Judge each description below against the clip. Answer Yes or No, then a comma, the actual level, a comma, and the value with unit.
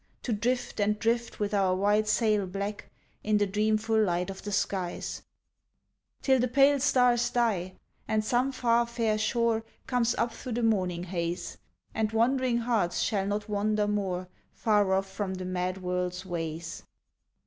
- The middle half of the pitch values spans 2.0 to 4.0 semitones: Yes, average, 3.6 semitones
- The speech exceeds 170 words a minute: No, average, 160 wpm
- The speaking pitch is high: Yes, high, 210 Hz